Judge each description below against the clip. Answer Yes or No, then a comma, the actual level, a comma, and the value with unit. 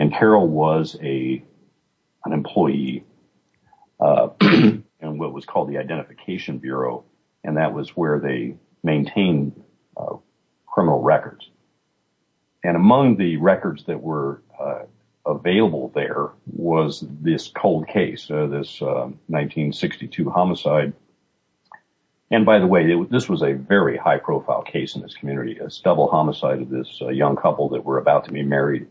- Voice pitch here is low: Yes, very low, 70 Hz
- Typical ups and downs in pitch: No, narrow, 2.2 semitones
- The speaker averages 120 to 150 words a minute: Yes, average, 140 wpm